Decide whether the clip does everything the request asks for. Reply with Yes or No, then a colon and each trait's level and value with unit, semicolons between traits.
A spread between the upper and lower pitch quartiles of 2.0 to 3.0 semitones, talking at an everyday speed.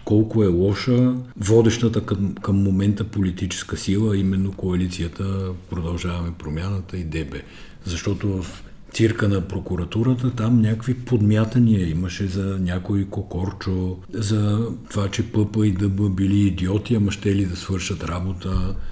Yes: narrow, 2.6 semitones; average, 130 wpm